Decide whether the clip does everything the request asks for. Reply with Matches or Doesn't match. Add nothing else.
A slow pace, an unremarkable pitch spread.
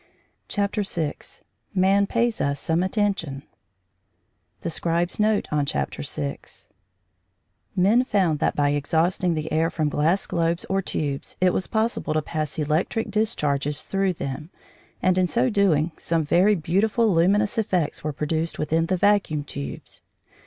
Doesn't match